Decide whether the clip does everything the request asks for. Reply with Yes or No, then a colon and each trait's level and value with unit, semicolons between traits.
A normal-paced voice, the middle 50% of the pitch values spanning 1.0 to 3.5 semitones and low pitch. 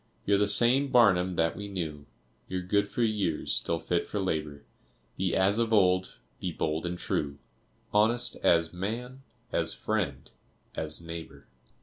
No: average, 150 wpm; average, 4.1 semitones; very low, 95 Hz